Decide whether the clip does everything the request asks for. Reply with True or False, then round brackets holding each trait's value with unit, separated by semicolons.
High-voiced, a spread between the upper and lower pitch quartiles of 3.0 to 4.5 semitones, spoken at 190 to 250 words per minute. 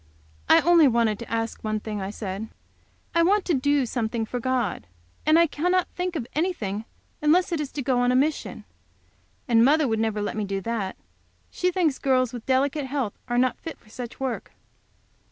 False (255 Hz; 5.4 semitones; 195 wpm)